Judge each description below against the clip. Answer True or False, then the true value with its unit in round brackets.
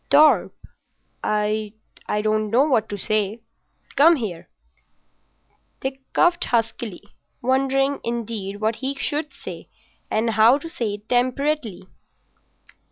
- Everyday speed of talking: False (110 wpm)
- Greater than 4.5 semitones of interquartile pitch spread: False (4.2 semitones)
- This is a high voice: True (235 Hz)